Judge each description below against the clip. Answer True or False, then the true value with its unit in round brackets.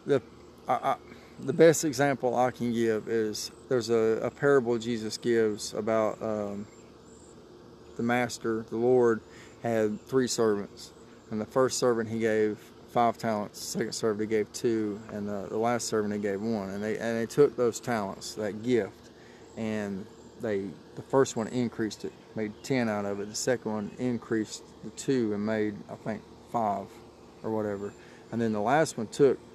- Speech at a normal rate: True (175 wpm)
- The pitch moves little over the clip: True (1.9 semitones)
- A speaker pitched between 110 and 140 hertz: True (115 Hz)